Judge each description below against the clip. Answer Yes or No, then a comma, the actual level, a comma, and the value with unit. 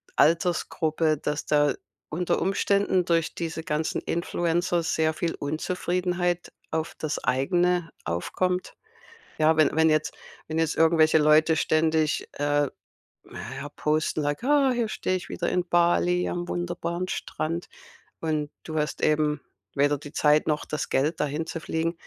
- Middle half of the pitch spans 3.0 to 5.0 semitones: No, narrow, 2.4 semitones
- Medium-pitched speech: Yes, medium, 160 Hz